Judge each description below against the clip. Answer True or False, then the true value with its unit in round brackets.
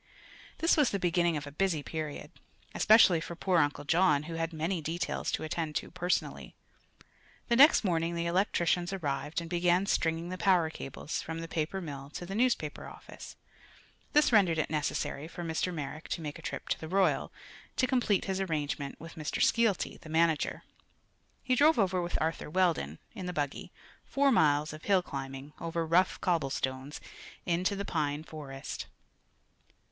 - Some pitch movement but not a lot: True (3.4 semitones)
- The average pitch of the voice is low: False (165 Hz)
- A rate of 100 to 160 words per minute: False (170 wpm)